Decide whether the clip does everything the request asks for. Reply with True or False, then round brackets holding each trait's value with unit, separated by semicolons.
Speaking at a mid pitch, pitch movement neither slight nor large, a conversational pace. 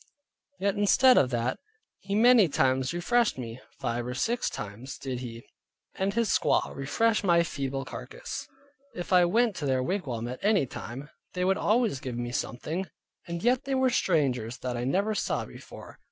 False (165 Hz; 8.4 semitones; 175 wpm)